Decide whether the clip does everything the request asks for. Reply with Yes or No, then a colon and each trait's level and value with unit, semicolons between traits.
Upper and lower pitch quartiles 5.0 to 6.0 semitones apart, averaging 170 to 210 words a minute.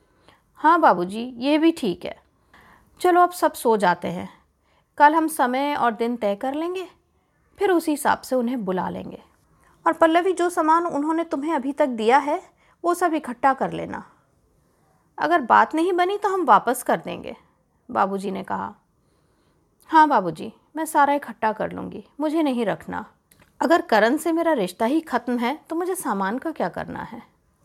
Yes: wide, 5.5 semitones; average, 175 wpm